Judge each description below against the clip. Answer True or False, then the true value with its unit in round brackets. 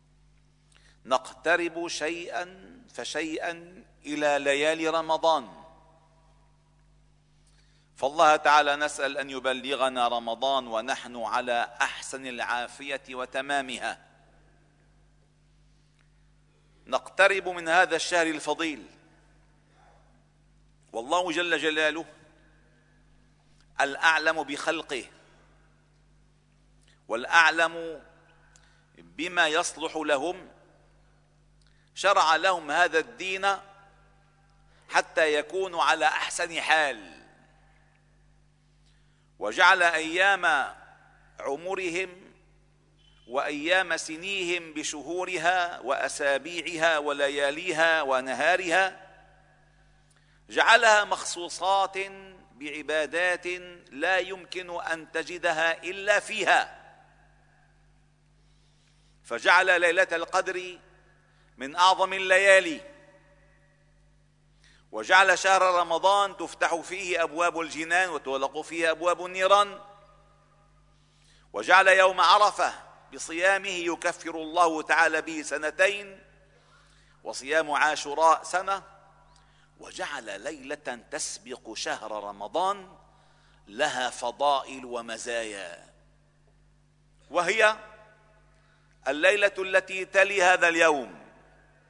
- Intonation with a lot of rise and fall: False (3.6 semitones)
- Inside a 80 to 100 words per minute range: False (65 wpm)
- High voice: False (160 Hz)